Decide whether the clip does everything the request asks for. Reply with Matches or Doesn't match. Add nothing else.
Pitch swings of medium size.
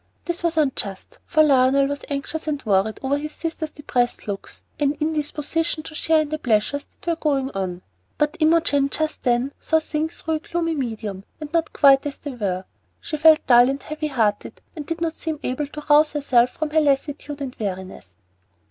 Matches